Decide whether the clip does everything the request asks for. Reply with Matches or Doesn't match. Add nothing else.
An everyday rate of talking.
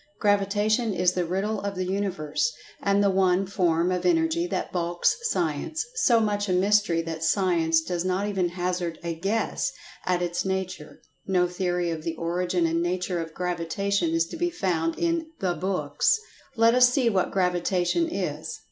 Matches